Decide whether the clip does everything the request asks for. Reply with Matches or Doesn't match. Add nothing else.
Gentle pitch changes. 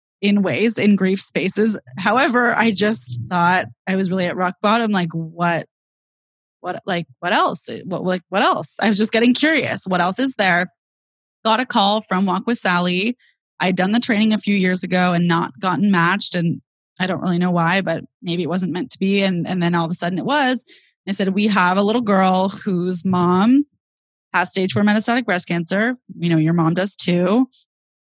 Doesn't match